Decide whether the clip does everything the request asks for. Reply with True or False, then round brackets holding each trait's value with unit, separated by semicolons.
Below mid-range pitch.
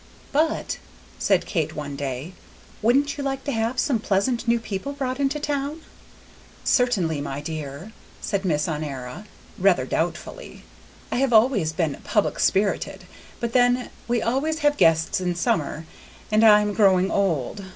False (210 Hz)